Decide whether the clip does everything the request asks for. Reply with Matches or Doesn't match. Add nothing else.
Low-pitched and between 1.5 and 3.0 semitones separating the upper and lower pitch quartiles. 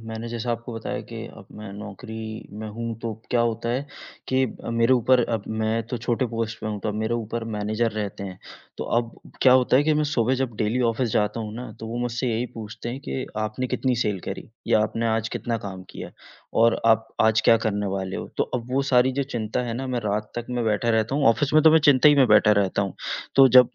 Matches